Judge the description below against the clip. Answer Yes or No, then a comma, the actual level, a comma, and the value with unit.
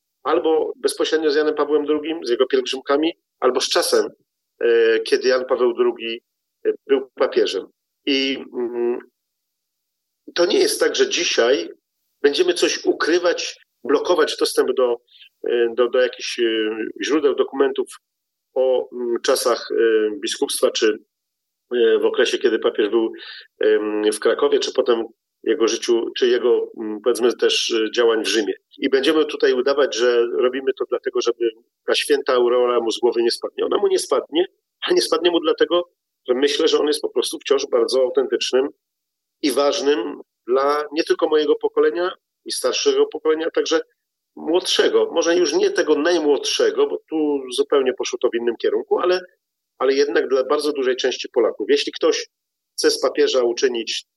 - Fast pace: No, average, 150 wpm